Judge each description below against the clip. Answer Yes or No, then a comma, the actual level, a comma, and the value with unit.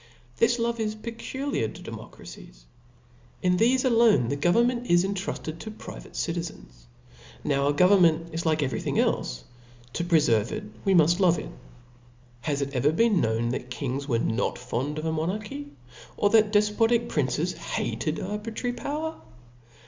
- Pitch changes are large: Yes, wide, 8.0 semitones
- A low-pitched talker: No, medium, 175 Hz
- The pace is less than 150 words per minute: No, average, 155 wpm